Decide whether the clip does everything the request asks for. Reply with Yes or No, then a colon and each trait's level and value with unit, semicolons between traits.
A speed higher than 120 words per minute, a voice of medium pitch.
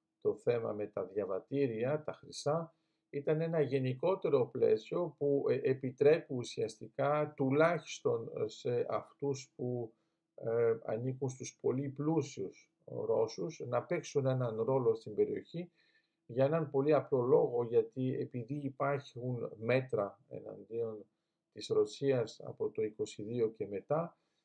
No: slow, 115 wpm; medium, 155 Hz